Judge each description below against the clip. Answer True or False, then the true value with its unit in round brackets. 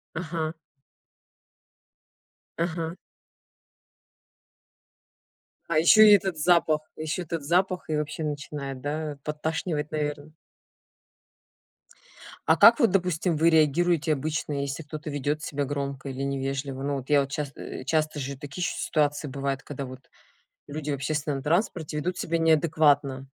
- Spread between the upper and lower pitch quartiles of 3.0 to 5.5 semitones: False (2.5 semitones)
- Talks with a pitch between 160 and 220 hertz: False (150 Hz)